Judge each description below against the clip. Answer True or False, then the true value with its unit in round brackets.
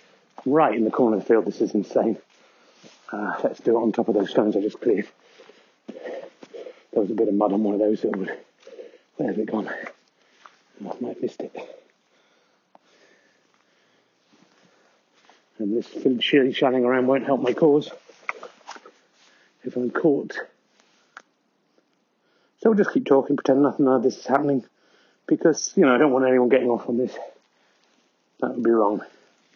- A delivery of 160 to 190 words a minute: True (170 wpm)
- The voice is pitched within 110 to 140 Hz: True (135 Hz)